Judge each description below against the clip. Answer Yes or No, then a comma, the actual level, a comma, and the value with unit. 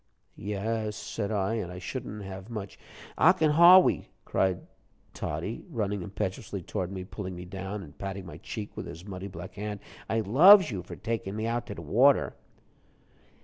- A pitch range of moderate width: Yes, average, 3.3 semitones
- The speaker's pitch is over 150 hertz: No, low, 100 Hz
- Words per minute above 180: No, average, 170 wpm